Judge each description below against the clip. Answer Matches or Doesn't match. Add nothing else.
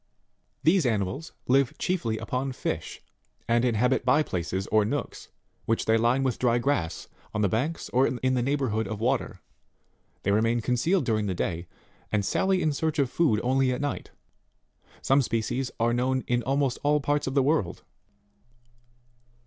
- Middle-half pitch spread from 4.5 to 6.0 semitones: Doesn't match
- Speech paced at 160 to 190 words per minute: Matches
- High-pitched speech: Doesn't match